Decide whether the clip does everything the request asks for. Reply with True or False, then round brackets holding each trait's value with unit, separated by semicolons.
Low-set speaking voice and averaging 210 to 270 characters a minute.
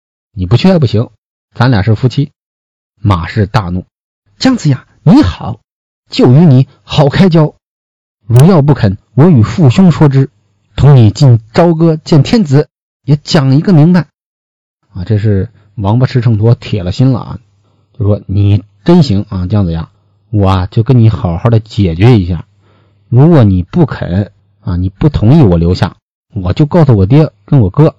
True (115 Hz; 225 characters per minute)